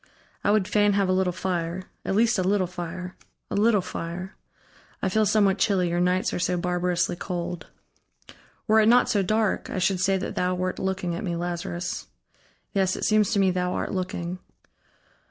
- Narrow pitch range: Yes, narrow, 2.0 semitones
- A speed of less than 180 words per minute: No, average, 190 wpm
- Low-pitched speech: No, medium, 185 Hz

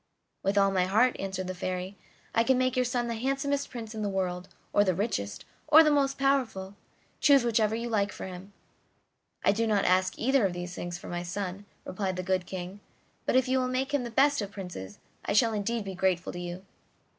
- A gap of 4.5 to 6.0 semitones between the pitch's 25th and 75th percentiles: Yes, average, 5.0 semitones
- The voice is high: Yes, high, 205 Hz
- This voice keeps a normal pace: No, fast, 220 wpm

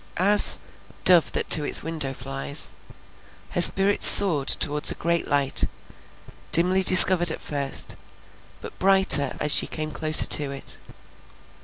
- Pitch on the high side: No, medium, 155 Hz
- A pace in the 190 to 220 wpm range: No, slow, 135 wpm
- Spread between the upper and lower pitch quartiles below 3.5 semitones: No, average, 4.4 semitones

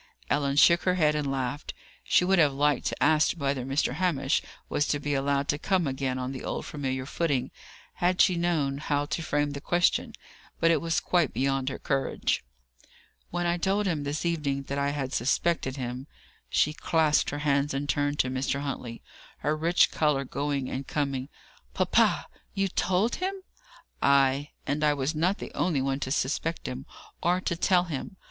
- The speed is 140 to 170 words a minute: No, average, 185 wpm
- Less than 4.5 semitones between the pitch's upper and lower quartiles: Yes, average, 3.4 semitones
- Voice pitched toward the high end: No, medium, 145 Hz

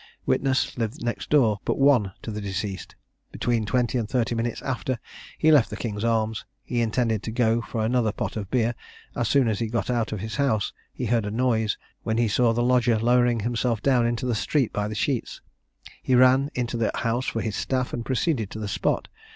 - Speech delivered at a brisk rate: Yes, fast, 215 wpm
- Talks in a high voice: No, low, 115 Hz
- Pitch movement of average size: No, narrow, 2.2 semitones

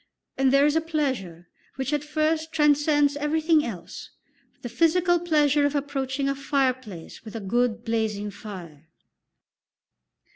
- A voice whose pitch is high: Yes, very high, 275 Hz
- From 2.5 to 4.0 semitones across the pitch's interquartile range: No, average, 5.2 semitones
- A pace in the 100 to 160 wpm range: Yes, slow, 135 wpm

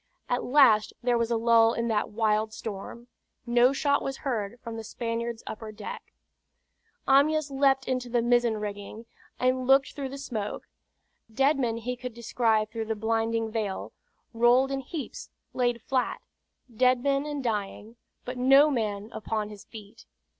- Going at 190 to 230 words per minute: No, average, 160 wpm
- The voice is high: Yes, high, 235 Hz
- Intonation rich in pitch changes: No, average, 3.0 semitones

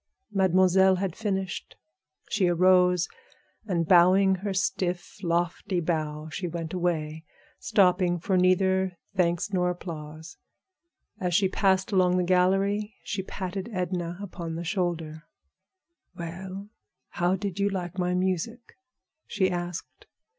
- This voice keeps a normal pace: No, slow, 120 wpm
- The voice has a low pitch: No, medium, 180 Hz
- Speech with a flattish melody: Yes, narrow, 1.6 semitones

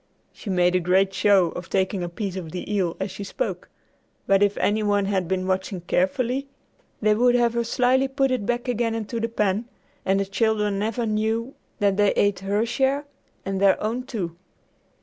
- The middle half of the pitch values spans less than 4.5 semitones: Yes, average, 3.6 semitones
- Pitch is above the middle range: Yes, high, 205 Hz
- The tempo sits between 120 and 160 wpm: No, average, 195 wpm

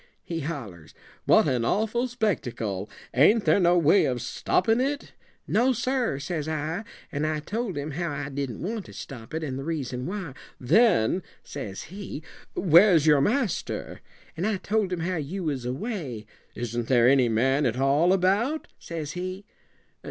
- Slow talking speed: No, average, 165 wpm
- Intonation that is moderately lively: No, wide, 6.9 semitones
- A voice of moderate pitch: Yes, medium, 160 Hz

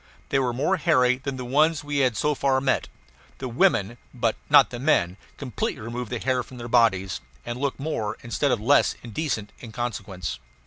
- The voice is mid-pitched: No, low, 125 Hz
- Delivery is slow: No, average, 190 wpm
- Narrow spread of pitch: No, average, 3.1 semitones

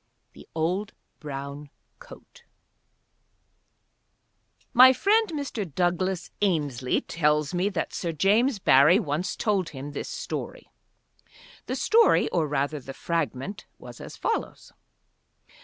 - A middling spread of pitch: No, wide, 5.9 semitones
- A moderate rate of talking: No, slow, 110 wpm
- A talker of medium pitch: Yes, medium, 175 Hz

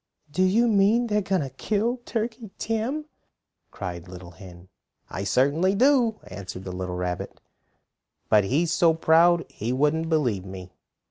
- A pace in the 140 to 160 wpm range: Yes, average, 155 wpm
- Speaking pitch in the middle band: Yes, medium, 160 Hz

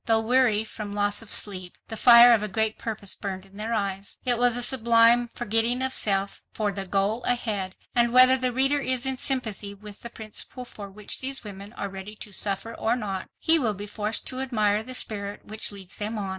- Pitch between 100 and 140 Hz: No, high, 220 Hz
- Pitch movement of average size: Yes, average, 3.2 semitones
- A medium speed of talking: No, fast, 215 wpm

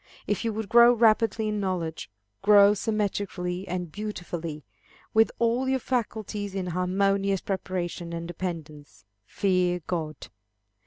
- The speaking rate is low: Yes, slow, 120 wpm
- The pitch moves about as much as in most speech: Yes, average, 3.4 semitones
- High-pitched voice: Yes, high, 195 Hz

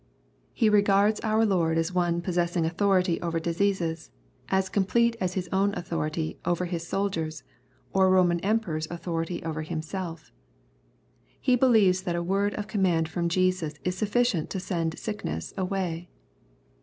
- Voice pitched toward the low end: No, medium, 180 Hz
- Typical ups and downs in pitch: Yes, average, 3.0 semitones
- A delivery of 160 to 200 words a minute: No, average, 150 wpm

